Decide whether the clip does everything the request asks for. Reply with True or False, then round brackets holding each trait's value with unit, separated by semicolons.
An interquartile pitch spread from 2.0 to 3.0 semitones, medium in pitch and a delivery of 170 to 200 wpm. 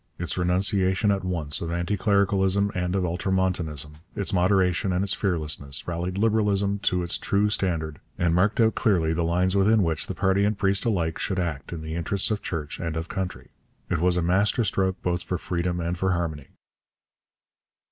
False (2.7 semitones; 90 Hz; 180 wpm)